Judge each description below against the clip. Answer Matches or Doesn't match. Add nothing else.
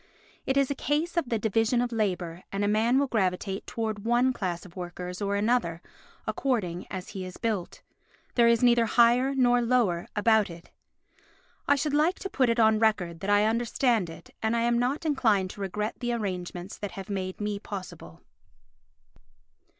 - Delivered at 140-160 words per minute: Doesn't match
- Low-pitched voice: Doesn't match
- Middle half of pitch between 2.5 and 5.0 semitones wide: Matches